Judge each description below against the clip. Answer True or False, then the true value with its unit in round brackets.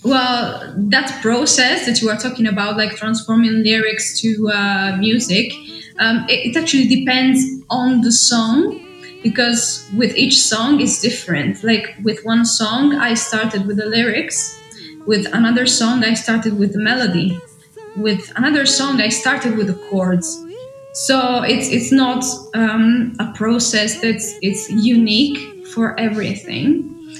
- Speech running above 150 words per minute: False (145 wpm)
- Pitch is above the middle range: True (230 Hz)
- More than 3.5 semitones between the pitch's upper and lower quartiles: False (3.0 semitones)